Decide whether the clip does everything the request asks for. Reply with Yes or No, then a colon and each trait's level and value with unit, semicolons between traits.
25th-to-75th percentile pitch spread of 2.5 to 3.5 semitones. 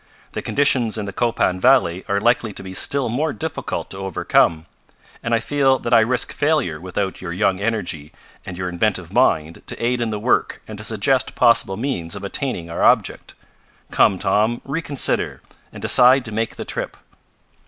No: average, 5.0 semitones